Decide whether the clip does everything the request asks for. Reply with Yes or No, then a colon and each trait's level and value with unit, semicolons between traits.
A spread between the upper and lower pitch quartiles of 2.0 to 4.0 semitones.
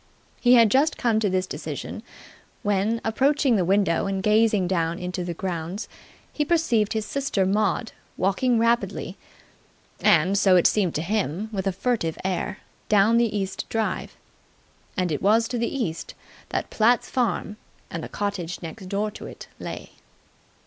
Yes: average, 3.7 semitones